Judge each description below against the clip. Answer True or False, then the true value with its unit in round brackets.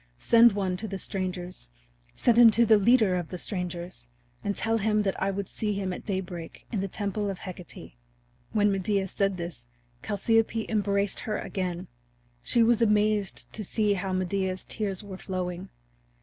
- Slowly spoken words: False (170 wpm)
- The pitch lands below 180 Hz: False (195 Hz)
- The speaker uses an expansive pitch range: False (2.5 semitones)